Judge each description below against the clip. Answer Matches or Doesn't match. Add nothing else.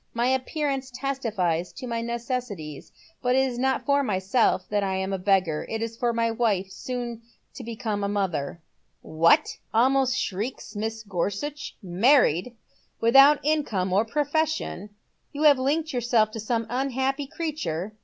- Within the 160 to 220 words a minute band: Matches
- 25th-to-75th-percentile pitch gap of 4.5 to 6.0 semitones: Matches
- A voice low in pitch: Doesn't match